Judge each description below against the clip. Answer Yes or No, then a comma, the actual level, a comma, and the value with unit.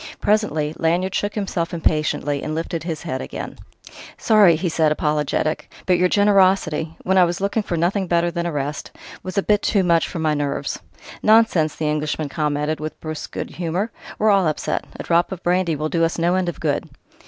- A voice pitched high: No, medium, 170 Hz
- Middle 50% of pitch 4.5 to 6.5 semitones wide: No, average, 3.4 semitones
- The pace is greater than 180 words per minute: Yes, average, 190 wpm